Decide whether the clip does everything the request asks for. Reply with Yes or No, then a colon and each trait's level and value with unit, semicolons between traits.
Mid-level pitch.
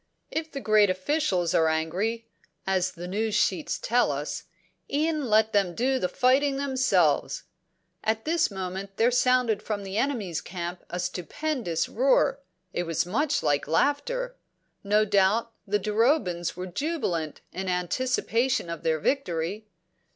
No: high, 210 Hz